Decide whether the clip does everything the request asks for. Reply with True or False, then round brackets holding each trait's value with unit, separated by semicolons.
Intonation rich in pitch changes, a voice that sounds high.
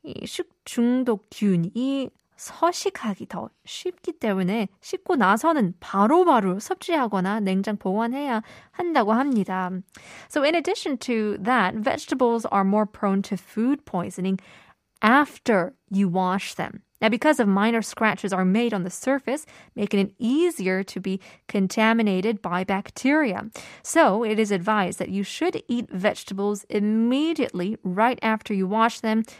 False (4.9 semitones; 220 Hz)